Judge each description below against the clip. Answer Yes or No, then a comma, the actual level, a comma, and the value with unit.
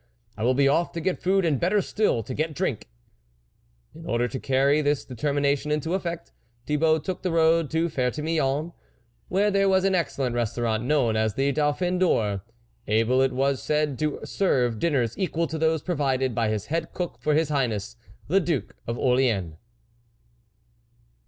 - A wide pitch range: No, average, 5.0 semitones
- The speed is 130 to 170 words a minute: No, average, 180 wpm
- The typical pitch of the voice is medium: Yes, medium, 145 Hz